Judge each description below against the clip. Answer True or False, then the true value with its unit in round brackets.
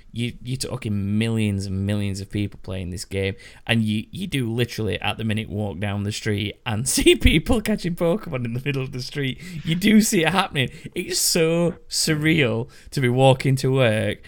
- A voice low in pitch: True (120 Hz)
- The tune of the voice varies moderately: False (7.2 semitones)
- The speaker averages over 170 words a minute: True (200 wpm)